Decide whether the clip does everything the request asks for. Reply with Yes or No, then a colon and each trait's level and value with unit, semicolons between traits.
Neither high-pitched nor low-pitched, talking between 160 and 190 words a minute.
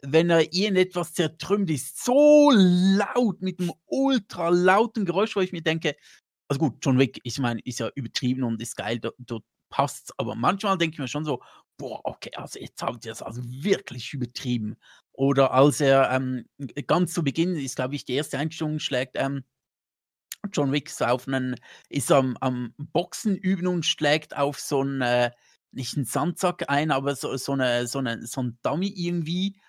Yes: medium, 145 Hz; average, 185 wpm